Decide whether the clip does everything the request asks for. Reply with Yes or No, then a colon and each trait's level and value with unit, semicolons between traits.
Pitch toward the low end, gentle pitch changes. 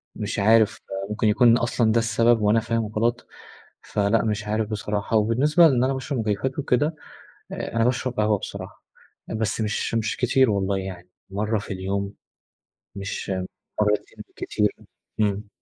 Yes: low, 110 Hz; narrow, 2.2 semitones